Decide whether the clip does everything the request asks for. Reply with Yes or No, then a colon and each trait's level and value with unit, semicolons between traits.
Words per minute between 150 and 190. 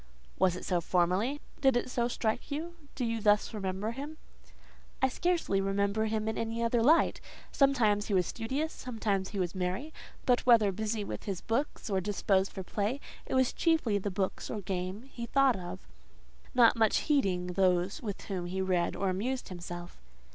Yes: average, 180 wpm